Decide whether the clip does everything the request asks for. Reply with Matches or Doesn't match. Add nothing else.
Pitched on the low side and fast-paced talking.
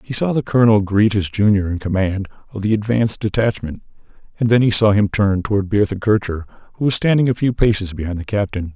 Matches